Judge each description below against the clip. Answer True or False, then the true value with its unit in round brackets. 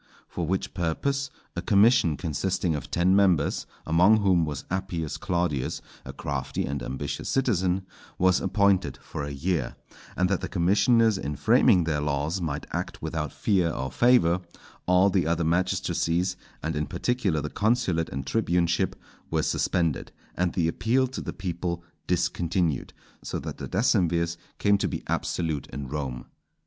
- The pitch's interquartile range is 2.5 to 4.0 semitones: True (3.4 semitones)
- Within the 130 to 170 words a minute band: True (155 wpm)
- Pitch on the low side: True (90 Hz)